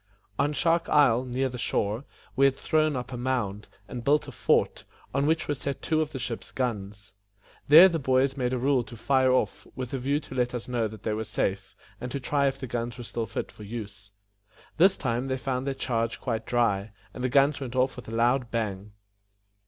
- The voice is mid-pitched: No, low, 125 Hz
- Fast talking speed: Yes, fast, 225 wpm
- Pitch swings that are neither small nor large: Yes, average, 3.0 semitones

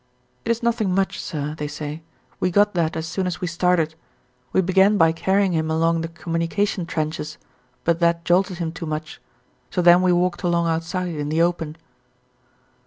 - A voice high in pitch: No, medium, 170 Hz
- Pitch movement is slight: Yes, narrow, 2.2 semitones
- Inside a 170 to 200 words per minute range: Yes, average, 180 wpm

